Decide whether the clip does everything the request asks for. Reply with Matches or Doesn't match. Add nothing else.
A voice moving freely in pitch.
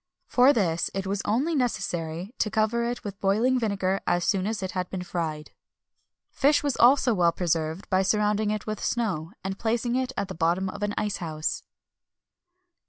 Doesn't match